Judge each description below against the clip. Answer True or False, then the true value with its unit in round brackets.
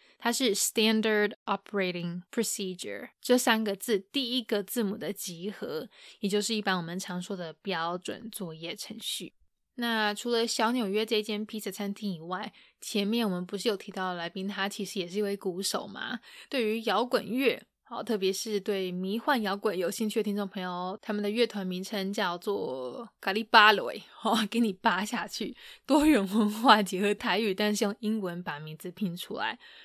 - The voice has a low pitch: False (210 Hz)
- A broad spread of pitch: False (2.7 semitones)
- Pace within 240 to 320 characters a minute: True (305 characters per minute)